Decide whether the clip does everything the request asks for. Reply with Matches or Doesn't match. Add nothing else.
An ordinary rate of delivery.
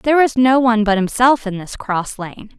Doesn't match